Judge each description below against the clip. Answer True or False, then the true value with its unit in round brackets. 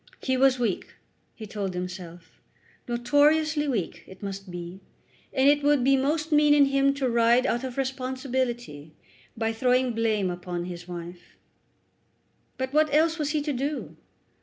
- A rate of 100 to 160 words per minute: True (155 wpm)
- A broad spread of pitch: True (6.5 semitones)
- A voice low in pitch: False (255 Hz)